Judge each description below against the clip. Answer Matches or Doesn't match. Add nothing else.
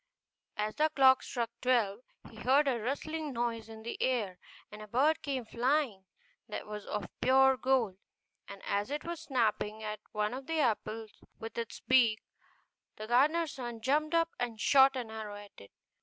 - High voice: Matches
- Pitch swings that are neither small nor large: Matches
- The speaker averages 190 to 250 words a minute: Doesn't match